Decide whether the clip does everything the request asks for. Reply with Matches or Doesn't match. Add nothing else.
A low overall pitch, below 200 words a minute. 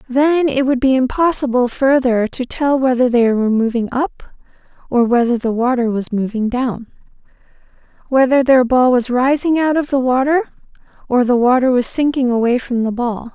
Doesn't match